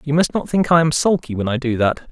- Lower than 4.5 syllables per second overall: No, 6.0 syllables/s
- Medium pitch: Yes, medium, 145 Hz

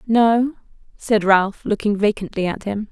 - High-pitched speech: Yes, high, 210 Hz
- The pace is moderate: Yes, average, 145 wpm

